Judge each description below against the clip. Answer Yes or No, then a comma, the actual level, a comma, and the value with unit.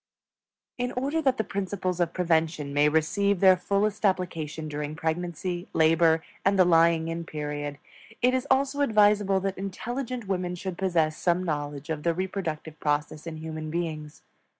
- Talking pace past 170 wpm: No, average, 155 wpm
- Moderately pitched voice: Yes, medium, 175 Hz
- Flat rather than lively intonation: No, average, 4.0 semitones